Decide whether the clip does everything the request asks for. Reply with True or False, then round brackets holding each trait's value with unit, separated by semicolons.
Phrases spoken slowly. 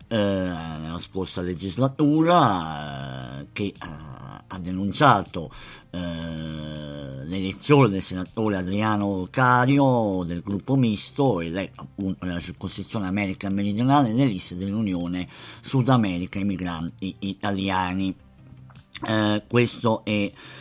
True (100 wpm)